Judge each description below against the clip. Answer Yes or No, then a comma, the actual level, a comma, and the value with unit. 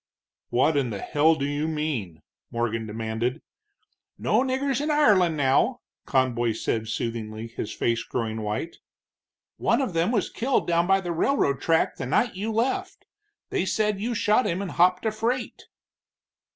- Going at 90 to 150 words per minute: No, average, 160 wpm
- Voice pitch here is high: No, medium, 160 Hz